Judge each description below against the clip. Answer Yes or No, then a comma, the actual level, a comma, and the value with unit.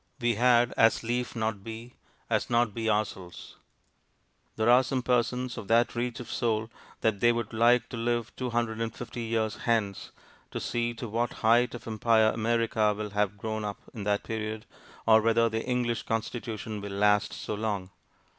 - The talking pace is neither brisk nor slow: Yes, average, 180 wpm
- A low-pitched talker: Yes, low, 115 Hz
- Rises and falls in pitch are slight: Yes, narrow, 1.6 semitones